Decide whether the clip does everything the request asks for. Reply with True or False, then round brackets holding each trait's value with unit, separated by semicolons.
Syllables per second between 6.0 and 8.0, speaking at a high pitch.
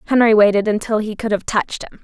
True (6.6 syllables/s; 215 Hz)